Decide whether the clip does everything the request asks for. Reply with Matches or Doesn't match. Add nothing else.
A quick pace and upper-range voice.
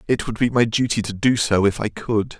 Doesn't match